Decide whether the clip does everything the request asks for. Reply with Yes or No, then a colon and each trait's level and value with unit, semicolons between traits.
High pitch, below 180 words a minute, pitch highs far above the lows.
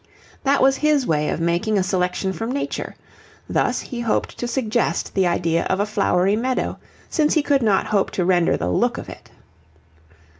No: high, 210 Hz; average, 185 wpm; wide, 6.0 semitones